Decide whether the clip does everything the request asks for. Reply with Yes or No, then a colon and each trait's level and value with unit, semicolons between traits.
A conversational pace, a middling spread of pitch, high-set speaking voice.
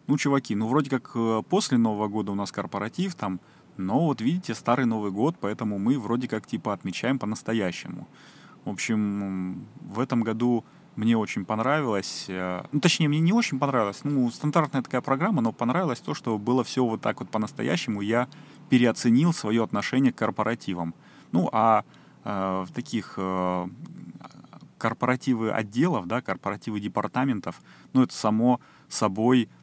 No: average, 150 wpm; average, 3.5 semitones; low, 115 Hz